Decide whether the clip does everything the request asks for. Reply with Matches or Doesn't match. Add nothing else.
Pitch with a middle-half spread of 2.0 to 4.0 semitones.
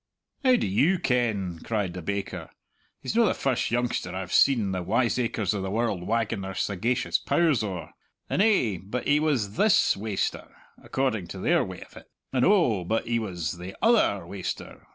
Doesn't match